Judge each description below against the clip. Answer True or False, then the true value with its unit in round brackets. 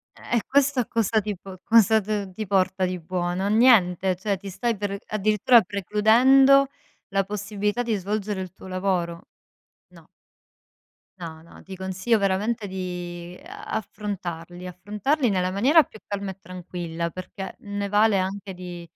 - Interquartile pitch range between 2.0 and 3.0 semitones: True (2.7 semitones)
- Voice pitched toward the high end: True (195 Hz)